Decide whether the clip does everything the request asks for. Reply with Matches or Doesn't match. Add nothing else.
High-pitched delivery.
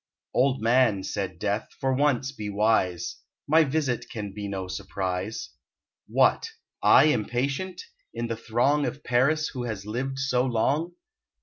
Doesn't match